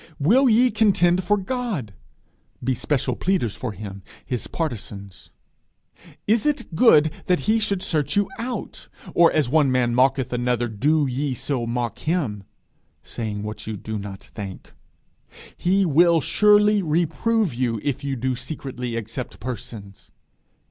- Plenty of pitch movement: Yes, wide, 7.6 semitones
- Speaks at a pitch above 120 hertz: Yes, medium, 140 Hz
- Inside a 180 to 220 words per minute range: No, average, 145 wpm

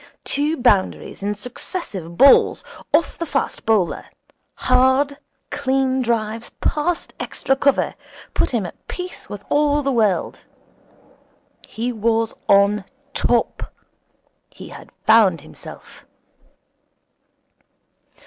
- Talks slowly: Yes, slow, 100 wpm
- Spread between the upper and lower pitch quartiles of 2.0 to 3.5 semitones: No, average, 4.9 semitones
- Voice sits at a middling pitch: No, high, 240 Hz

